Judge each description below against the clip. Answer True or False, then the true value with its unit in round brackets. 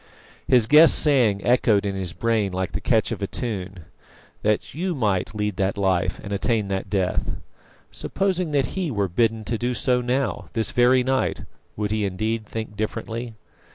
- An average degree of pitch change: True (3.8 semitones)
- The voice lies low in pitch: True (110 Hz)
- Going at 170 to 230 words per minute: True (175 wpm)